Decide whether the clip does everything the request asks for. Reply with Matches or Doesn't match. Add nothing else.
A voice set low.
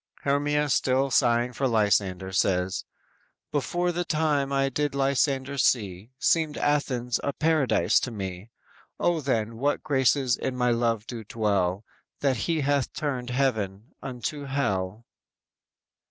Matches